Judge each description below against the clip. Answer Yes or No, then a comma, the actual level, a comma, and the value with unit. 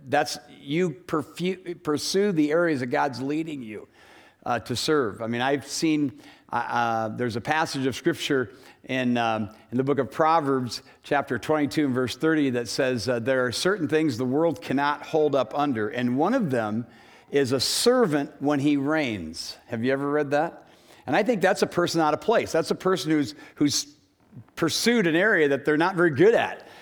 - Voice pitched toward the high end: No, medium, 145 Hz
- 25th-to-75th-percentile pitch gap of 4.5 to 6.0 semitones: No, average, 3.9 semitones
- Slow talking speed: No, average, 195 wpm